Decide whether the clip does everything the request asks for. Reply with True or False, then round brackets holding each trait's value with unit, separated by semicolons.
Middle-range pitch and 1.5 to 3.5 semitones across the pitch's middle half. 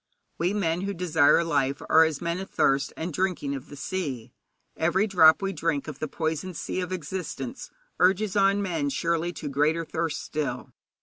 False (165 Hz; 3.9 semitones)